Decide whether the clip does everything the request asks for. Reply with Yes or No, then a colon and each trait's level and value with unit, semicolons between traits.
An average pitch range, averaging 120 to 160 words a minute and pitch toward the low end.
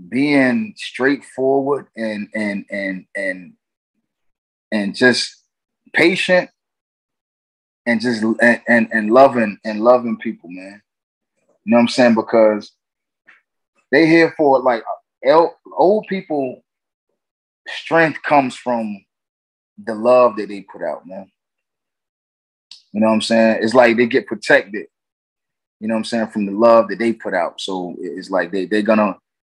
Yes: average, 3.5 semitones; average, 140 wpm; low, 115 Hz